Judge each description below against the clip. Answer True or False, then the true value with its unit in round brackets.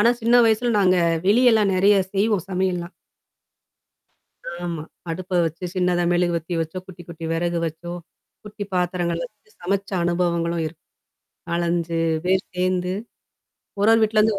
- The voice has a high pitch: False (180 Hz)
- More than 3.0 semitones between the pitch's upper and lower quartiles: False (2.7 semitones)